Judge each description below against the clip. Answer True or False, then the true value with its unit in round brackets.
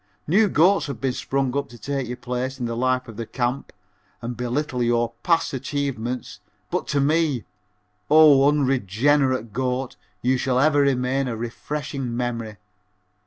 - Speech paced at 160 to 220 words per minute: False (150 wpm)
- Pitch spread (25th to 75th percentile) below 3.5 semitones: True (2.7 semitones)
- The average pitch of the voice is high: False (130 Hz)